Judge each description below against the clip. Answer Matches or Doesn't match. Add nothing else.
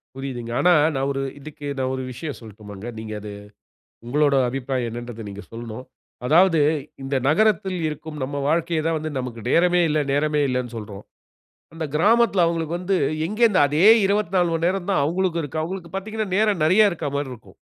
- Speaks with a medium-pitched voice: Matches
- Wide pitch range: Matches